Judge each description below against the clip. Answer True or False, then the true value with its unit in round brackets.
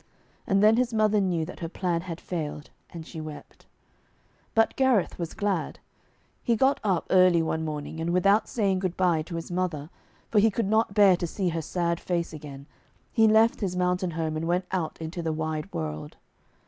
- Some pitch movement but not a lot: True (3.7 semitones)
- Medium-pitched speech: True (180 Hz)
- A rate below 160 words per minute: False (195 wpm)